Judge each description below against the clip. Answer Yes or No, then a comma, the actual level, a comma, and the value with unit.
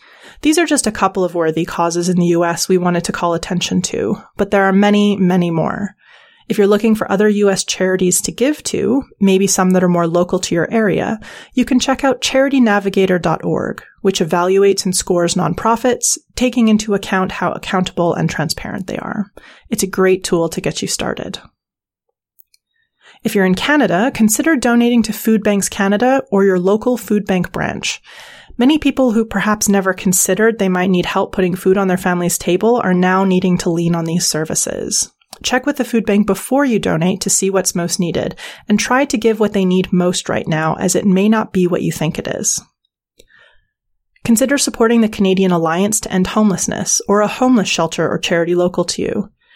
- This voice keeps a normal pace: Yes, average, 195 wpm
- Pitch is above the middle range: Yes, high, 195 Hz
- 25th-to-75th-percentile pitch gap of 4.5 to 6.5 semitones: No, average, 3.9 semitones